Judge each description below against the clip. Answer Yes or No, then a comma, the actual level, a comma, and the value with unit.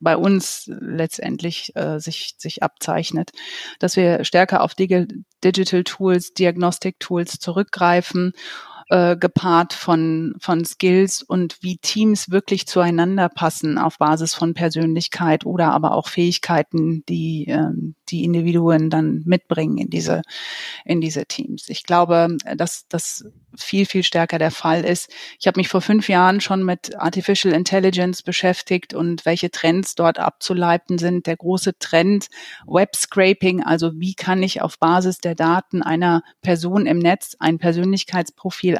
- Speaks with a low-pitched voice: No, medium, 175 Hz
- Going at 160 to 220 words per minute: No, average, 145 wpm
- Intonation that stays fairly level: Yes, narrow, 2.0 semitones